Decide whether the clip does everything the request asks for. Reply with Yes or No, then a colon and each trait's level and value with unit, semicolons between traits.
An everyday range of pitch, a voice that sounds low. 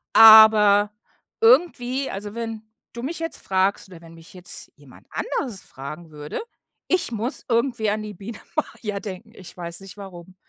No: average, 4.0 semitones; high, 210 Hz